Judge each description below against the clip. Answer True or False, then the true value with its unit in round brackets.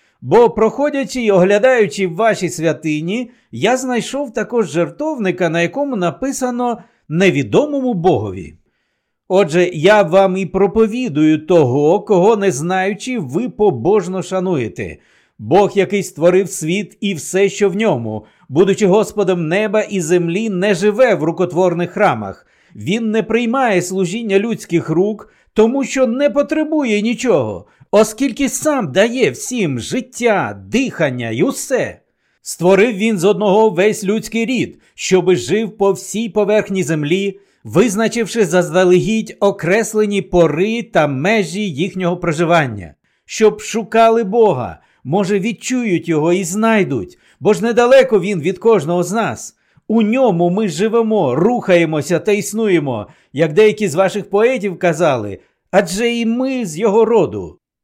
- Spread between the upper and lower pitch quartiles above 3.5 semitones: True (4.0 semitones)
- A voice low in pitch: False (200 Hz)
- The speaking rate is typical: True (125 wpm)